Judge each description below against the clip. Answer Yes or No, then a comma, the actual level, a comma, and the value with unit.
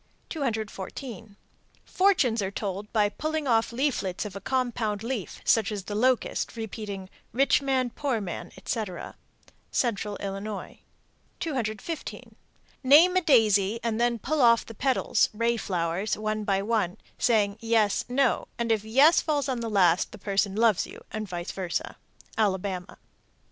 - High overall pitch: Yes, high, 220 Hz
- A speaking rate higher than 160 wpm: No, average, 145 wpm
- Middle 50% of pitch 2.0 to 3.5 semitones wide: No, average, 3.9 semitones